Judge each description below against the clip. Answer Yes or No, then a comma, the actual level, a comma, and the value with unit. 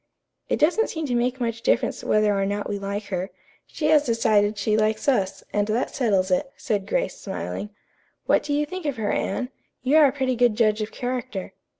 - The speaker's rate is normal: No, fast, 210 wpm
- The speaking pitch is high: Yes, high, 230 Hz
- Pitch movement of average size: Yes, average, 4.5 semitones